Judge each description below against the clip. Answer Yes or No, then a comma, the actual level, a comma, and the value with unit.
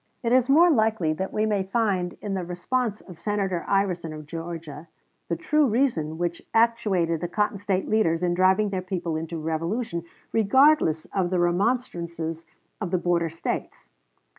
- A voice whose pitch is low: No, medium, 185 Hz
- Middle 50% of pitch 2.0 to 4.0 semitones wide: No, average, 4.4 semitones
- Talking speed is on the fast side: No, average, 165 wpm